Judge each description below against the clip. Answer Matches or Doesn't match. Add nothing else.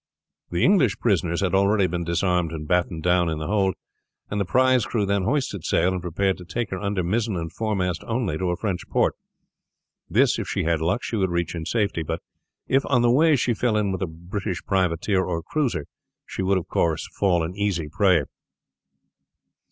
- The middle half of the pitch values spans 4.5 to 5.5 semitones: Doesn't match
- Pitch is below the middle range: Matches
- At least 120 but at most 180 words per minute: Doesn't match